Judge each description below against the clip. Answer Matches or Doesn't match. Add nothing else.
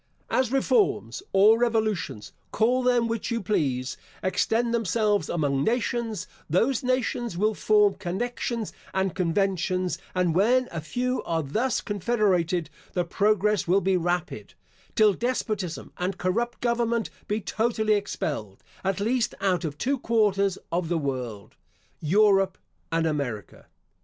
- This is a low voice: Doesn't match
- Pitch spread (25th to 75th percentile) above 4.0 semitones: Matches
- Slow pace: Matches